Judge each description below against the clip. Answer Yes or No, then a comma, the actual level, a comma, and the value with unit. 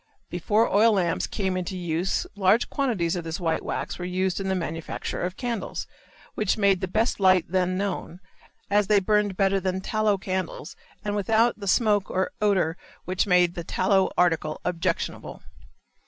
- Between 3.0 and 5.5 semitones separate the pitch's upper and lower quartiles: No, narrow, 2.4 semitones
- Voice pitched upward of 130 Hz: Yes, high, 190 Hz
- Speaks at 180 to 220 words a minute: No, average, 170 wpm